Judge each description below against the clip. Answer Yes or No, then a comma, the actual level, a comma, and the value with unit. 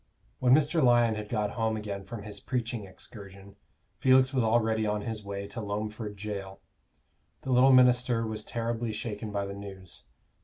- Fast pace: No, average, 165 wpm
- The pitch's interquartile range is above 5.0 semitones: No, average, 2.8 semitones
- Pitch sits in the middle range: No, low, 110 Hz